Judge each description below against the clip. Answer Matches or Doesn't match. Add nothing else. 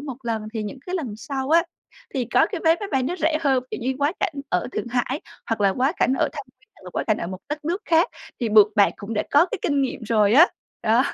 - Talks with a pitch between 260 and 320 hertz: Matches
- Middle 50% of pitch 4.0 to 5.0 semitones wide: Doesn't match